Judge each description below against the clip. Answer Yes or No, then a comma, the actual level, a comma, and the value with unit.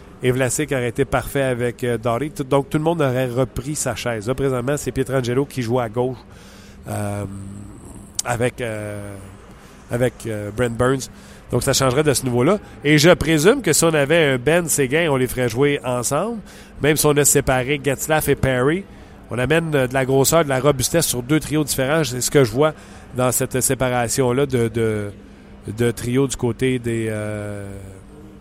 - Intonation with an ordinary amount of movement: Yes, average, 4.3 semitones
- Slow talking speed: No, average, 190 wpm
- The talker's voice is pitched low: Yes, low, 125 Hz